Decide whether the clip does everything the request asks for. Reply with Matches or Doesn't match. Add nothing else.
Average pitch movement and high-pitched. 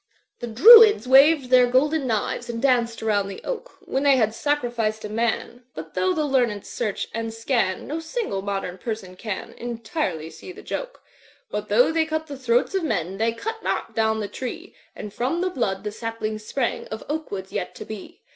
Doesn't match